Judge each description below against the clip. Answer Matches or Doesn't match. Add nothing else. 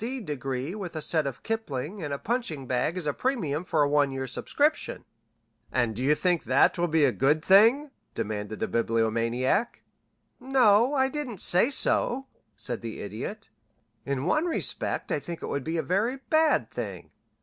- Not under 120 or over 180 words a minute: Matches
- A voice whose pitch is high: Doesn't match